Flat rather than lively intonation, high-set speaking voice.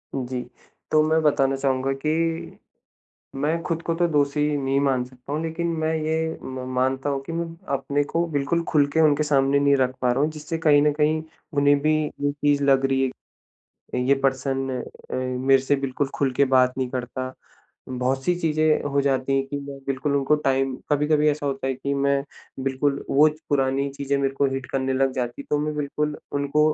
No: narrow, 2.1 semitones; medium, 140 Hz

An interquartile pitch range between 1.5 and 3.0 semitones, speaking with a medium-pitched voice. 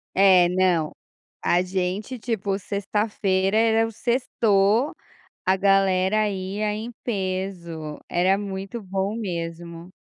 No: narrow, 2.4 semitones; high, 195 Hz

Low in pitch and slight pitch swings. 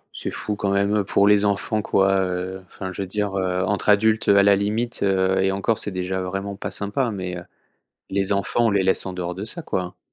Yes: low, 100 Hz; narrow, 1.5 semitones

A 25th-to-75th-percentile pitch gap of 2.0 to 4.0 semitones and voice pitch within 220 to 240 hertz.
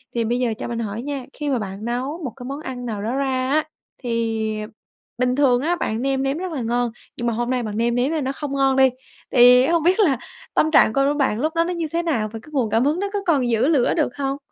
No: average, 3.6 semitones; very high, 260 Hz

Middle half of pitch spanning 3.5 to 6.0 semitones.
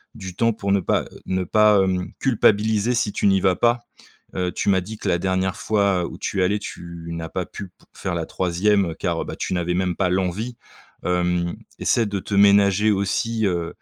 No: narrow, 2.6 semitones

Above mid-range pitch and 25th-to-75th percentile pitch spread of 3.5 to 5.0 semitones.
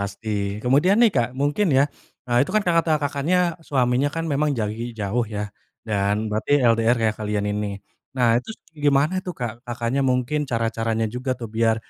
No: low, 120 Hz; average, 4.3 semitones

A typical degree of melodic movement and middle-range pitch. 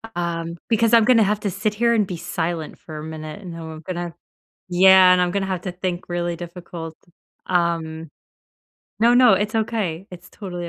Yes: average, 3.3 semitones; medium, 180 Hz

